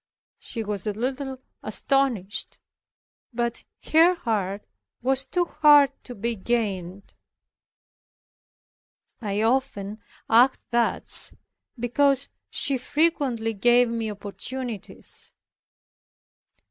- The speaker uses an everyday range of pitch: Yes, average, 4.1 semitones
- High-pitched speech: Yes, high, 240 Hz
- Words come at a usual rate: No, slow, 85 wpm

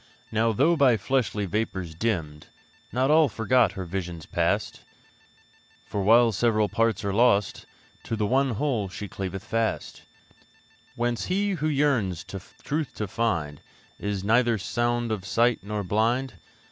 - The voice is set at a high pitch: No, low, 110 Hz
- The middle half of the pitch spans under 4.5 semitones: Yes, average, 3.9 semitones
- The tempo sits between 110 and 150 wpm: Yes, average, 145 wpm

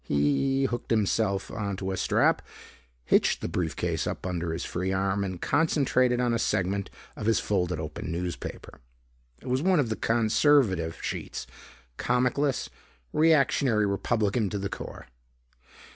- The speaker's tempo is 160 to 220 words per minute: No, average, 145 wpm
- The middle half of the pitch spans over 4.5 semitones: Yes, average, 5.1 semitones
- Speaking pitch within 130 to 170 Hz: No, low, 105 Hz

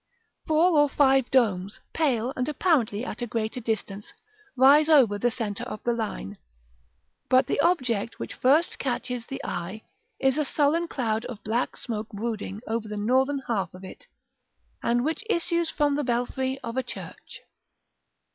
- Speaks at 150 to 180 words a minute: Yes, average, 160 wpm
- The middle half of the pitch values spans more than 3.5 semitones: Yes, average, 4.5 semitones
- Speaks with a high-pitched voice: Yes, high, 245 Hz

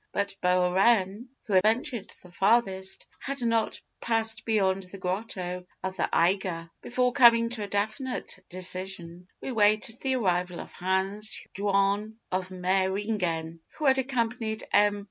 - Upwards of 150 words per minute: No, average, 140 wpm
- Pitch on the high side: Yes, high, 200 Hz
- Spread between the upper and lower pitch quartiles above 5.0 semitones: No, average, 3.5 semitones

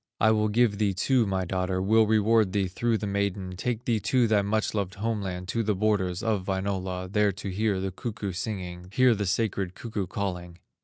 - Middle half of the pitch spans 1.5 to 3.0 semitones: Yes, average, 2.7 semitones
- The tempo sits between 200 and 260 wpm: Yes, fast, 205 wpm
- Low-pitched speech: Yes, low, 100 Hz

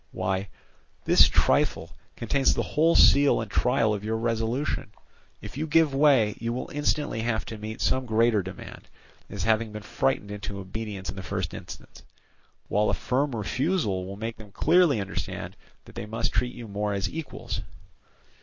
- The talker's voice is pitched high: No, low, 110 Hz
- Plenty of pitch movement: No, average, 4.5 semitones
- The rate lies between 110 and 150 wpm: No, average, 170 wpm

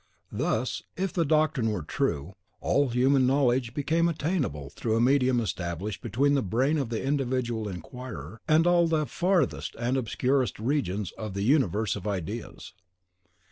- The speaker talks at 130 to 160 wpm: Yes, average, 150 wpm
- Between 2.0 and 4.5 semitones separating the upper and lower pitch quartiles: No, average, 5.1 semitones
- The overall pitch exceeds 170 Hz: No, low, 125 Hz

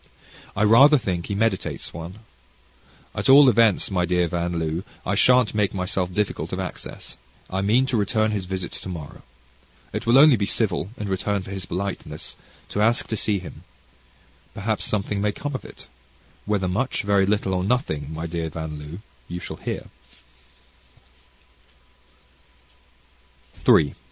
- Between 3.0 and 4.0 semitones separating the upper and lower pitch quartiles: Yes, average, 3.5 semitones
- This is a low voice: Yes, low, 100 Hz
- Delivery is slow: No, average, 150 wpm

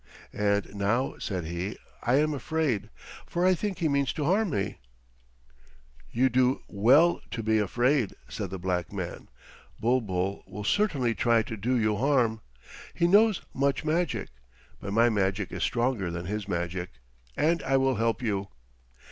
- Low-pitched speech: Yes, low, 115 Hz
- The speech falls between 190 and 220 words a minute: No, average, 155 wpm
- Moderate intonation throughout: No, wide, 5.8 semitones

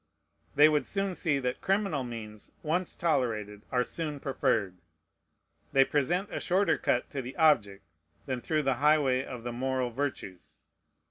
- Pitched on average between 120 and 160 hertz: Yes, low, 135 Hz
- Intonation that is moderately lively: Yes, average, 4.2 semitones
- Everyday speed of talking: Yes, average, 150 wpm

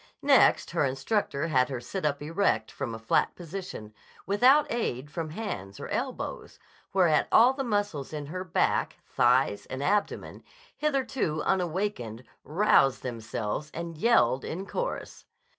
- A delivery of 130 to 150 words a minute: Yes, average, 140 wpm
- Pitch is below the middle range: No, medium, 155 Hz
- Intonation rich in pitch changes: Yes, wide, 7.8 semitones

